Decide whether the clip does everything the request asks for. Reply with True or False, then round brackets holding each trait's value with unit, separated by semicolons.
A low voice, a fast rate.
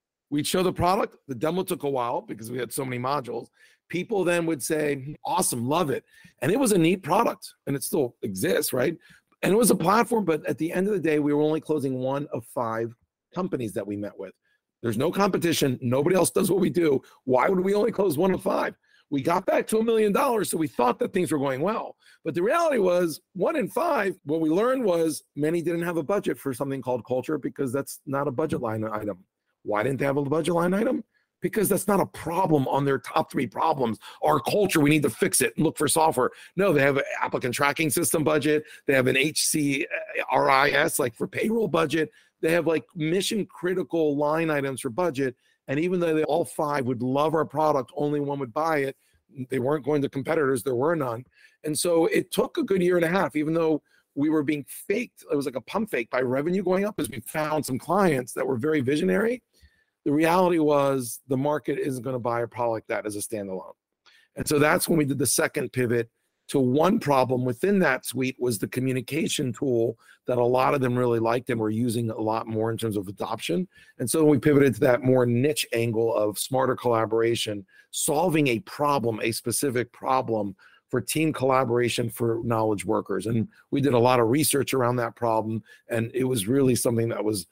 False (145 Hz; 220 wpm)